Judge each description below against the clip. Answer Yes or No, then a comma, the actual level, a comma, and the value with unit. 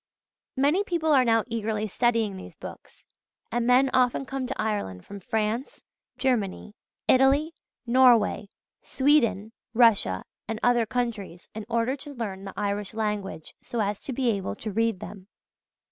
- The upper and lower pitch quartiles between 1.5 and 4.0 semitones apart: Yes, average, 3.7 semitones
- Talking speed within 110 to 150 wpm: Yes, average, 145 wpm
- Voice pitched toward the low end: No, high, 230 Hz